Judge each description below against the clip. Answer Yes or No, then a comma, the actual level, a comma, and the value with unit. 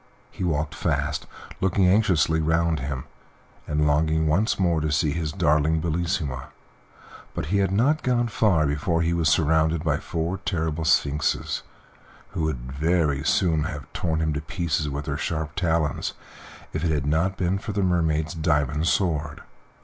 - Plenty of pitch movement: No, narrow, 2.6 semitones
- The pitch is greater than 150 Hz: No, very low, 80 Hz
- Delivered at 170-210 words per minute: No, average, 160 wpm